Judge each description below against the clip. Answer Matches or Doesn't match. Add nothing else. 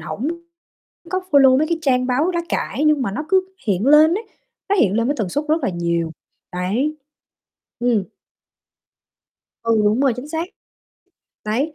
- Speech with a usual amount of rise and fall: Doesn't match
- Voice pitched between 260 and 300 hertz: Matches